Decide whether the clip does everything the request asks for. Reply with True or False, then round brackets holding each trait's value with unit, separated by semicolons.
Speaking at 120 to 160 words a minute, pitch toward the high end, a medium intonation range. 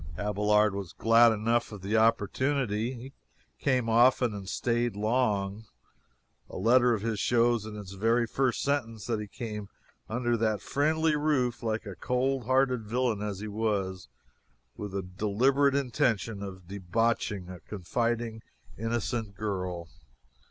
False (140 wpm; 115 Hz; 3.0 semitones)